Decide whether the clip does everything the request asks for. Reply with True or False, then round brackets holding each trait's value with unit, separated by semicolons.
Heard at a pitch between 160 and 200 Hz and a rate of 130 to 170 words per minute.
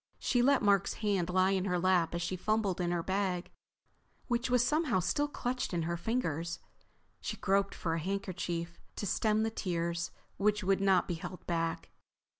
False (190 Hz; 180 wpm)